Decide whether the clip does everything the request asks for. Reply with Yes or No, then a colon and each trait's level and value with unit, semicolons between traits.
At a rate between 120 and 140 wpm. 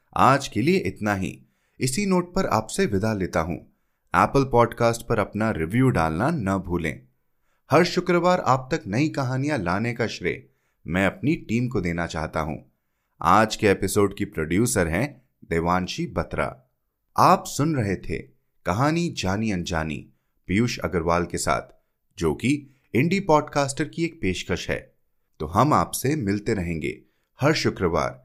Yes: average, 135 wpm